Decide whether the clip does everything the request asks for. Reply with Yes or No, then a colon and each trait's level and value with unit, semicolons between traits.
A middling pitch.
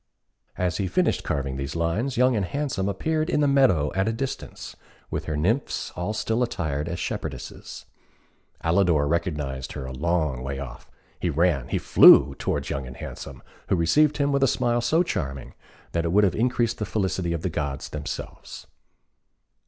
No: very low, 90 Hz